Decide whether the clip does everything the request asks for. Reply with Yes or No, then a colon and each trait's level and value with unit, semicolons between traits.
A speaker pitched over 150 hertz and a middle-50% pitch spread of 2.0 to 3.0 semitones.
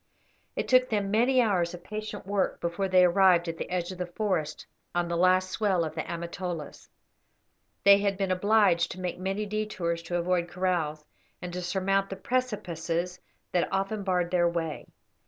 Yes: medium, 185 Hz; narrow, 2.5 semitones